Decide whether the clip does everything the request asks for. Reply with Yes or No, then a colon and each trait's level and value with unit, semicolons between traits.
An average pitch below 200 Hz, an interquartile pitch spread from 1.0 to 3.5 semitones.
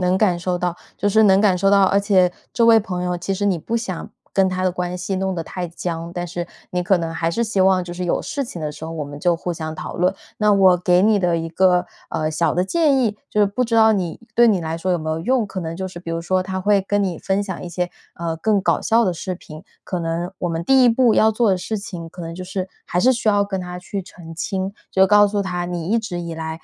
Yes: medium, 185 Hz; average, 2.8 semitones